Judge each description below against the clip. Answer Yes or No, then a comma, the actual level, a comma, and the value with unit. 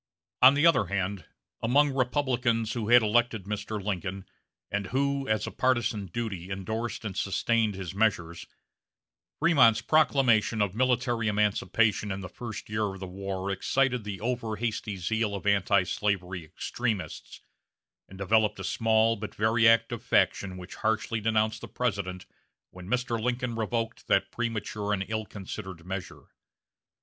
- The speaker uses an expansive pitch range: No, average, 3.2 semitones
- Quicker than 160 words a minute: No, average, 145 wpm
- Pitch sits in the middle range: No, low, 110 Hz